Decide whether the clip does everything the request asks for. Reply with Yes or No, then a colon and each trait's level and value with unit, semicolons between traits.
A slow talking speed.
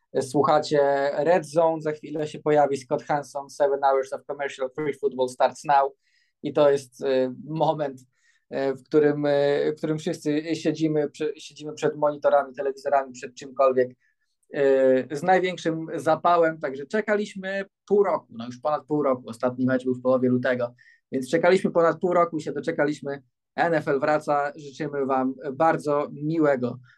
No: average, 145 wpm